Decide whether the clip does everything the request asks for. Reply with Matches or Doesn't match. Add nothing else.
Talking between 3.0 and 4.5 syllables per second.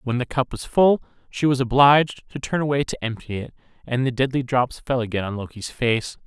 Doesn't match